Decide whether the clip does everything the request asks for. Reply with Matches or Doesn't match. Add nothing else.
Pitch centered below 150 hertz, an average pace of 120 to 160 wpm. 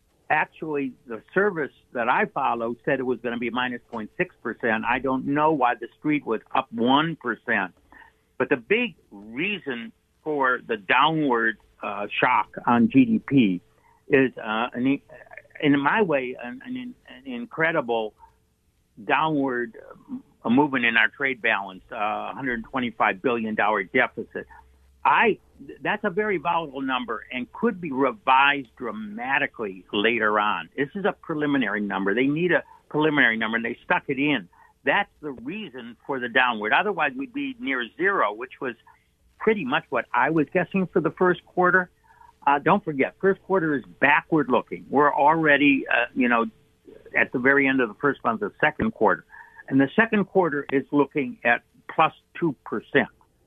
Matches